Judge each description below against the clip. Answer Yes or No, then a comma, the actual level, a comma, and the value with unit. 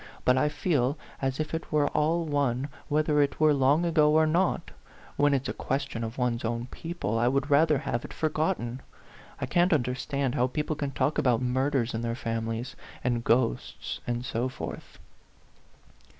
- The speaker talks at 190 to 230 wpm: No, average, 175 wpm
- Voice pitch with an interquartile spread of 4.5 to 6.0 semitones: No, average, 3.8 semitones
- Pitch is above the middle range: No, low, 135 Hz